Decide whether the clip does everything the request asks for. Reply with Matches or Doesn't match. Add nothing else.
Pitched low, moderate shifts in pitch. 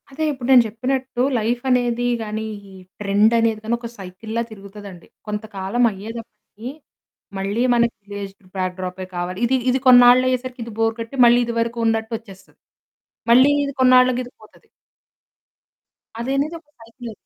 Doesn't match